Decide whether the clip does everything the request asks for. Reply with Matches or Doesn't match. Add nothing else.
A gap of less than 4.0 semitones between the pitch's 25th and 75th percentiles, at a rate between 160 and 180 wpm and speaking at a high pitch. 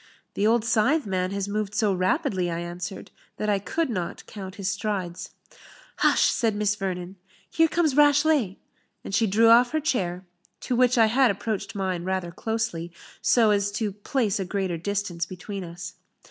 Matches